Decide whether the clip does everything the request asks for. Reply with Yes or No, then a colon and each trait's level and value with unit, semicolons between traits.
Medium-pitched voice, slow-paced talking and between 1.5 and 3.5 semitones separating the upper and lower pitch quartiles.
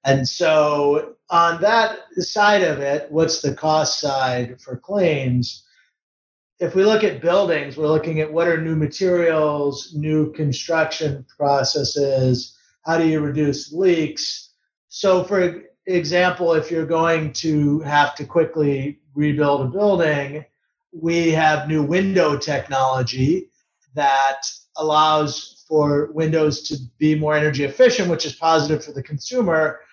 Yes: medium, 155 Hz; slow, 130 wpm; average, 2.8 semitones